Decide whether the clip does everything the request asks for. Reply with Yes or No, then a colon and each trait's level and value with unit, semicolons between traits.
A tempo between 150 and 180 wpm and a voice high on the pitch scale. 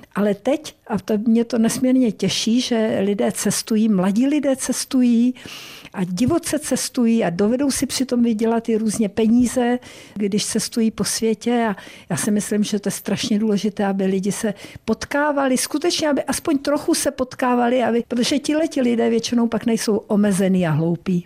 Yes: average, 165 wpm; high, 230 Hz